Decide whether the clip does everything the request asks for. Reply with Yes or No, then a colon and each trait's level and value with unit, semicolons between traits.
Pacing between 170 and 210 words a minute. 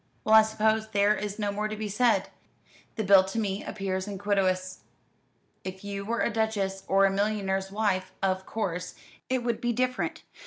Yes: average, 180 wpm